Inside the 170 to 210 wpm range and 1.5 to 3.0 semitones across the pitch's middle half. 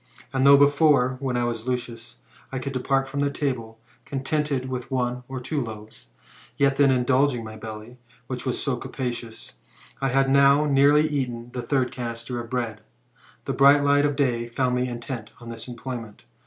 Yes: average, 180 wpm; narrow, 2.6 semitones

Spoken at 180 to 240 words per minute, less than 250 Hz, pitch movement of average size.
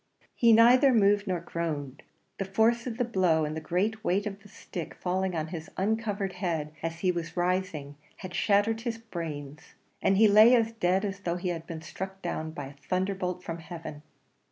Yes: average, 200 wpm; medium, 185 Hz; average, 4.0 semitones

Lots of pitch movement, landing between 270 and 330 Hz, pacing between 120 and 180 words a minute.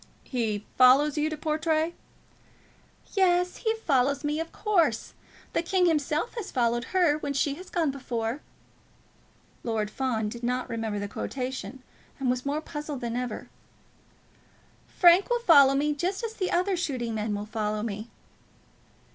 Yes: wide, 5.9 semitones; very high, 280 Hz; average, 150 wpm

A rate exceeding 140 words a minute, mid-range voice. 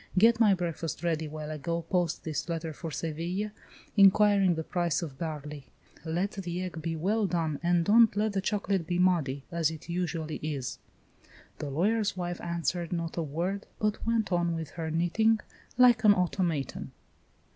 Yes: average, 170 wpm; medium, 175 Hz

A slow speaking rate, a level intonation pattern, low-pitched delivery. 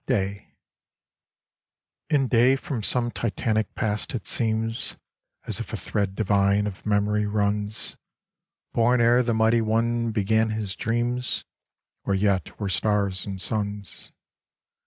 Yes: slow, 125 wpm; narrow, 2.3 semitones; low, 110 Hz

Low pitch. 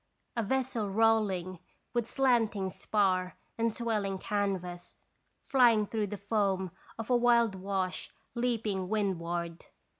No: high, 205 Hz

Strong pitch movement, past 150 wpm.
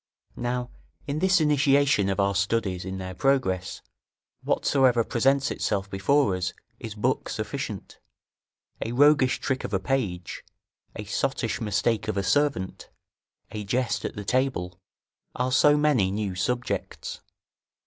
No: wide, 5.9 semitones; slow, 135 wpm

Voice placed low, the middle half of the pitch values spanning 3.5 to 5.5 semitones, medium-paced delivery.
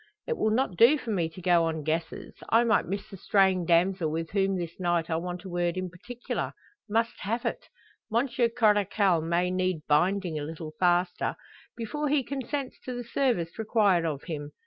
No: medium, 185 Hz; average, 5.1 semitones; average, 190 wpm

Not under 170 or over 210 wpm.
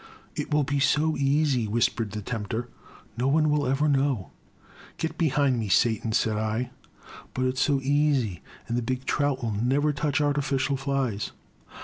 Yes: average, 185 wpm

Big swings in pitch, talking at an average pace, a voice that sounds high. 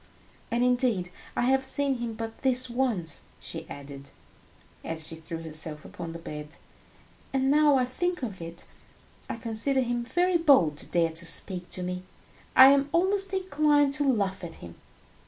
Yes: wide, 8.5 semitones; average, 170 wpm; high, 235 Hz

